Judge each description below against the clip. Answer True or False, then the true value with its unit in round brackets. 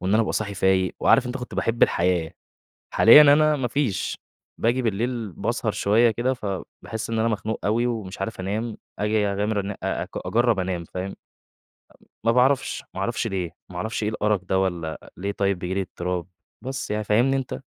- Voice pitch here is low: True (105 Hz)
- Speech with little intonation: False (3.8 semitones)